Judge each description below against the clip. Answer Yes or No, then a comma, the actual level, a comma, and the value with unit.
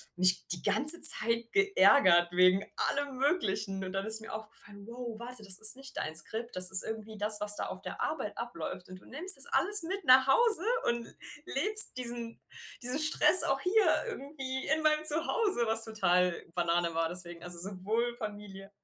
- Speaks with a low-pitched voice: No, high, 225 Hz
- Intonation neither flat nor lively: No, wide, 6.6 semitones